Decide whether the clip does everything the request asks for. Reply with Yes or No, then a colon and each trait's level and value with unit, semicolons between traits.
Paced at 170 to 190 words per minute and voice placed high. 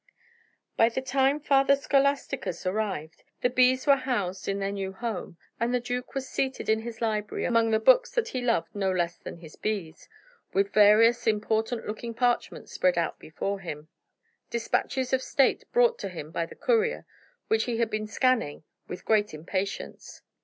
Yes: average, 175 wpm; high, 225 Hz